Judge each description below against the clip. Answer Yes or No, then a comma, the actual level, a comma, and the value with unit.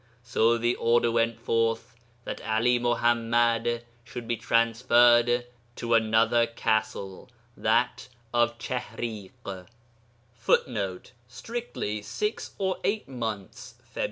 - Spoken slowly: Yes, slow, 100 wpm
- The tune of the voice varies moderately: No, narrow, 1.1 semitones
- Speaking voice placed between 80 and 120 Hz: Yes, low, 115 Hz